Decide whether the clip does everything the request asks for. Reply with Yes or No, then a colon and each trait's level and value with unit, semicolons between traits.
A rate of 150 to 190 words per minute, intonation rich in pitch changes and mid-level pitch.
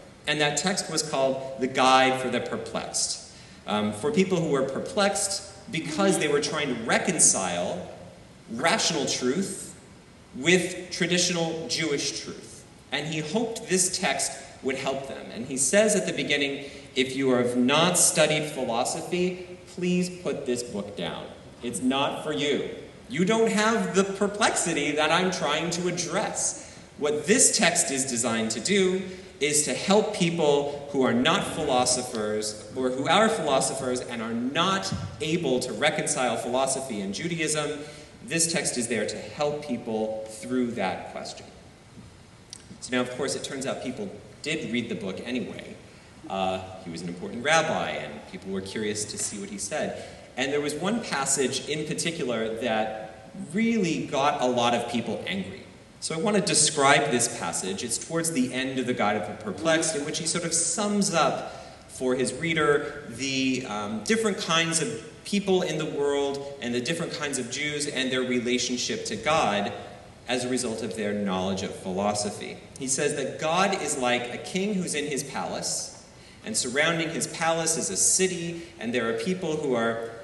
Yes: average, 170 wpm; wide, 5.9 semitones; medium, 145 Hz